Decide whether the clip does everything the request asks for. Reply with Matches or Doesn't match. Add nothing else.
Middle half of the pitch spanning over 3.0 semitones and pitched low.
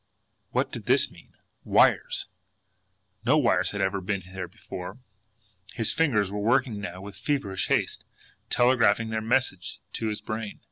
Matches